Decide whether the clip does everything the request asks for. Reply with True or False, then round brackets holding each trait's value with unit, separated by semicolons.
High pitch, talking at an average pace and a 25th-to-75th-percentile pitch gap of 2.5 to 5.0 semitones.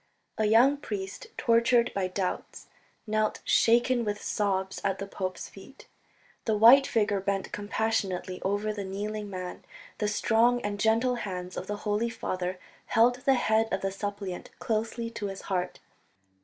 True (210 Hz; 155 wpm; 2.8 semitones)